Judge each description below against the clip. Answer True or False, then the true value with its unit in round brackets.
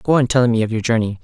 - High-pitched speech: False (115 Hz)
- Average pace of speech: False (340 wpm)